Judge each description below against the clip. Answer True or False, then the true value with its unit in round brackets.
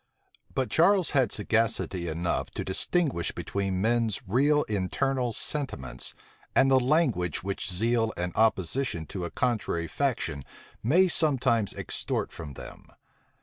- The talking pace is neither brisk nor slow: False (125 wpm)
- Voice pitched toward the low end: True (115 Hz)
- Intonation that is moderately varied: False (6.8 semitones)